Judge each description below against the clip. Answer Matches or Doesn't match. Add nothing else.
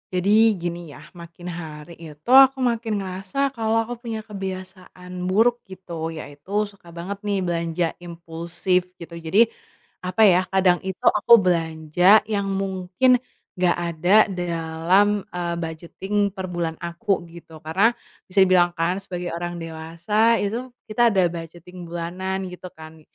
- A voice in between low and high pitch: Matches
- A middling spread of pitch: Matches